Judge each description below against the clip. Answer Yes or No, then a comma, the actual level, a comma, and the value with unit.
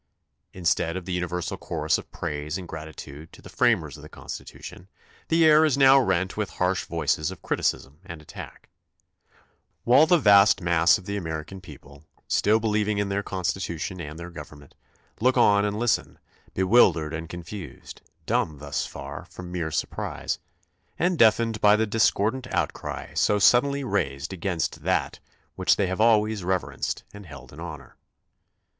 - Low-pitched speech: Yes, very low, 95 Hz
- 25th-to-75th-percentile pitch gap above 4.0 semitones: Yes, average, 4.7 semitones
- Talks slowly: No, average, 160 wpm